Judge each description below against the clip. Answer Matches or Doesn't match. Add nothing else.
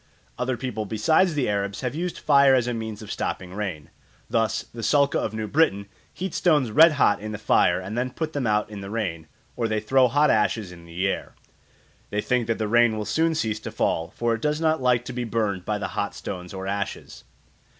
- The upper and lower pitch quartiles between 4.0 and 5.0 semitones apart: Matches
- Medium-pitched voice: Doesn't match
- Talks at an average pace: Doesn't match